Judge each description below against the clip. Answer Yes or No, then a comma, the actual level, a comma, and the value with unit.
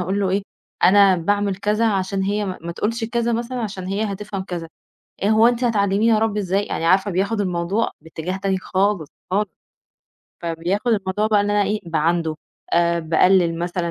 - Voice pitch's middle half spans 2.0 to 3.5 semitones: Yes, average, 2.8 semitones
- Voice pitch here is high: Yes, high, 195 Hz